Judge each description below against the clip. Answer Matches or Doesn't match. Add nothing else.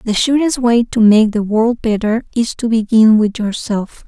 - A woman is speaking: Matches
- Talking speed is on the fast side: Doesn't match